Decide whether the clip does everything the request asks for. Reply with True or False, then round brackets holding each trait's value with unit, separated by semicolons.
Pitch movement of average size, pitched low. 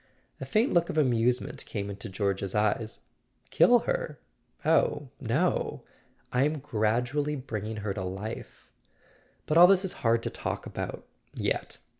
False (6.2 semitones; 120 Hz)